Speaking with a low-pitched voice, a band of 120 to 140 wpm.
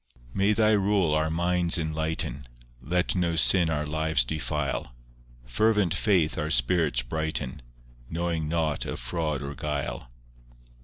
Yes: very low, 80 Hz; slow, 135 wpm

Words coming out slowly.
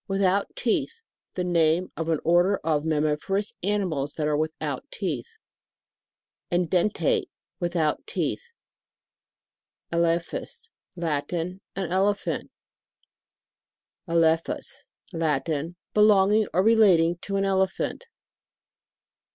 Yes: slow, 95 wpm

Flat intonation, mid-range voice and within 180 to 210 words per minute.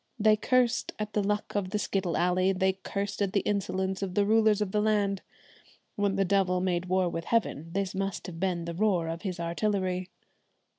No: narrow, 2.2 semitones; high, 195 Hz; average, 200 wpm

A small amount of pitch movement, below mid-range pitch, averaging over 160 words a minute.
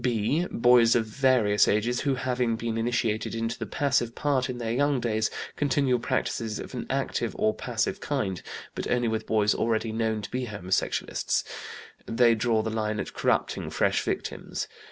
Yes: narrow, 2.3 semitones; low, 115 Hz; average, 170 wpm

